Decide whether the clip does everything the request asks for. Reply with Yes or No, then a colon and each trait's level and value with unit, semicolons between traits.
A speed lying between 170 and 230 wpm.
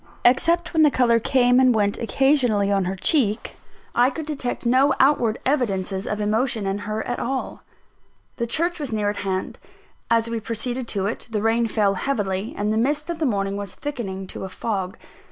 Yes: average, 190 wpm